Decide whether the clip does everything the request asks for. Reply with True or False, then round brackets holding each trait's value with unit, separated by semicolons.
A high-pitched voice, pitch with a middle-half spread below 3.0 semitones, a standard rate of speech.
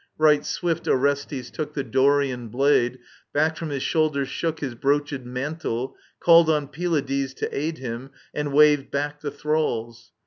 False (145 Hz; 2.6 semitones; 160 wpm)